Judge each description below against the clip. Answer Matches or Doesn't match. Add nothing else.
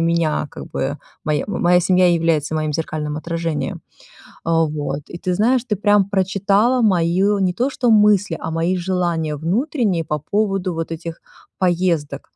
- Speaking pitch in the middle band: Matches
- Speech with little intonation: Doesn't match